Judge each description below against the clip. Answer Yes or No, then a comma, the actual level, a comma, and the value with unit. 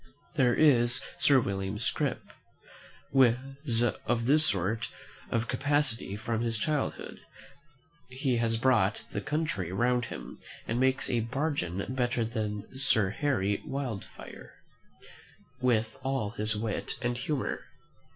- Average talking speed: No, slow, 120 wpm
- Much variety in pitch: No, average, 3.3 semitones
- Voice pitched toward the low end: Yes, low, 120 Hz